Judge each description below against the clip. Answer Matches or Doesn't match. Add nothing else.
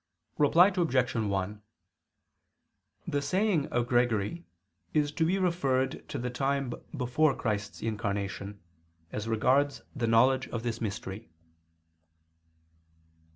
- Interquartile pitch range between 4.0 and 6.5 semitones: Matches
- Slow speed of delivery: Matches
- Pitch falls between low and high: Doesn't match